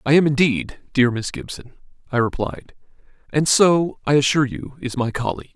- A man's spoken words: Yes, male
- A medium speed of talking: Yes, average, 175 wpm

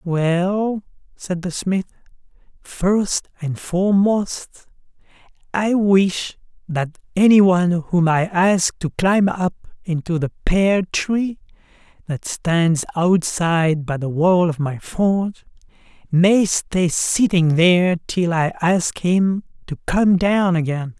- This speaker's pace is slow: Yes, slow, 125 wpm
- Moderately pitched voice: Yes, medium, 180 Hz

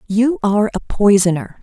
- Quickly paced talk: No, average, 150 wpm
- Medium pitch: No, high, 215 Hz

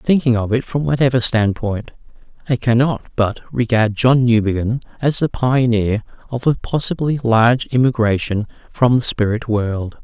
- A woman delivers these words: No, male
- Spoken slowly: No, average, 145 wpm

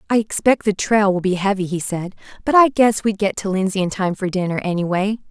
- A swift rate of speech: Yes, fast, 235 wpm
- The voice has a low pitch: No, high, 200 Hz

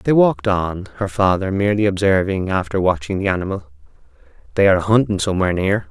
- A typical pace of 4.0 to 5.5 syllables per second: No, 6.4 syllables/s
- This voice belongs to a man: Yes, male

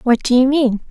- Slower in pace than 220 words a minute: No, fast, 265 wpm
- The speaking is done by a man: No, female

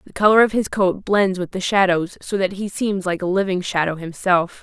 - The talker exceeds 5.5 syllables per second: No, 5.1 syllables/s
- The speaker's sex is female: Yes, female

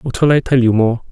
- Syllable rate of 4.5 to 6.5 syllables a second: Yes, 5.8 syllables/s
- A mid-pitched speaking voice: No, low, 125 Hz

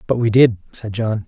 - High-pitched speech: No, low, 110 Hz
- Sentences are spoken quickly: Yes, fast, 235 wpm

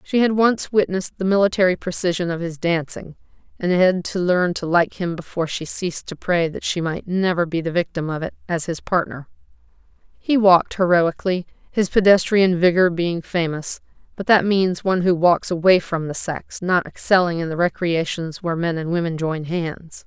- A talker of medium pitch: Yes, medium, 175 Hz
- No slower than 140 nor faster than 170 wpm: No, average, 190 wpm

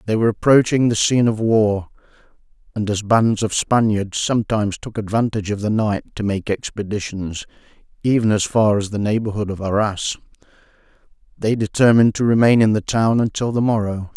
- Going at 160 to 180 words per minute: Yes, average, 165 wpm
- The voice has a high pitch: No, low, 110 Hz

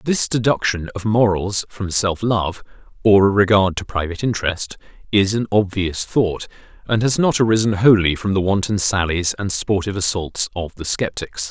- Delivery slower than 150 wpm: No, average, 165 wpm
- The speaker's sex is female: No, male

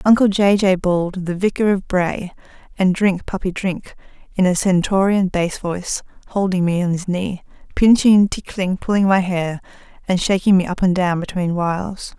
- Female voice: Yes, female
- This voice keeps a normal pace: Yes, average, 170 wpm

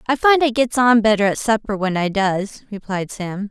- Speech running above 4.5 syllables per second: Yes, 4.9 syllables/s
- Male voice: No, female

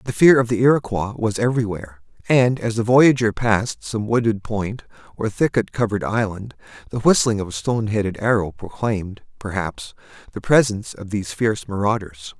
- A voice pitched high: No, low, 110 Hz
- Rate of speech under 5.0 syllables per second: No, 5.6 syllables/s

